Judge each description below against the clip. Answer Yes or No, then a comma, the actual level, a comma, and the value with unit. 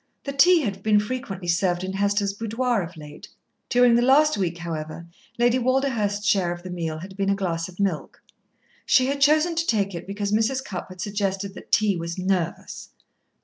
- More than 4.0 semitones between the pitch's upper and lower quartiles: Yes, average, 5.2 semitones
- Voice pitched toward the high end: Yes, high, 200 Hz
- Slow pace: No, average, 190 wpm